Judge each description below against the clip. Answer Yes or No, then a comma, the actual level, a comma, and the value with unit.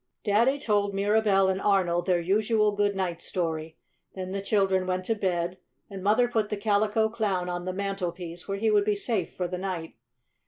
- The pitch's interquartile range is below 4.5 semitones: Yes, narrow, 2.4 semitones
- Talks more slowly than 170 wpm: No, average, 190 wpm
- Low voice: No, high, 195 Hz